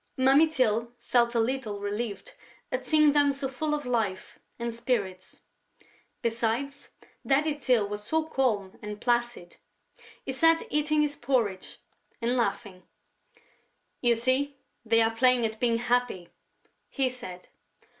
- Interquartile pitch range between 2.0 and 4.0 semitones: Yes, average, 3.7 semitones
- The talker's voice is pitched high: Yes, high, 240 Hz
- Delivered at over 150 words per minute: No, slow, 135 wpm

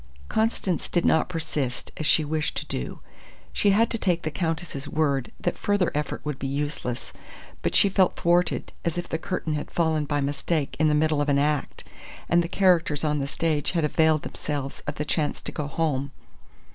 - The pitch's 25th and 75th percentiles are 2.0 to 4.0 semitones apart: Yes, average, 2.8 semitones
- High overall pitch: No, medium, 155 Hz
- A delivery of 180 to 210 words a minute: Yes, average, 195 wpm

